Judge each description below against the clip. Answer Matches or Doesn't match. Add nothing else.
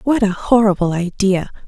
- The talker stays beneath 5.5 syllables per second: Matches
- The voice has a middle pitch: Doesn't match